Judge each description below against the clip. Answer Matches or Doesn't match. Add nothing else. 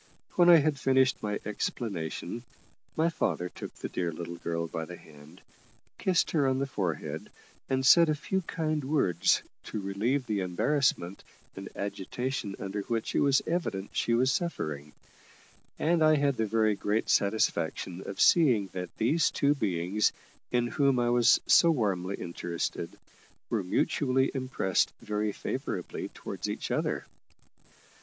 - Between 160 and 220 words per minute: Doesn't match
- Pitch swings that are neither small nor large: Doesn't match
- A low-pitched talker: Matches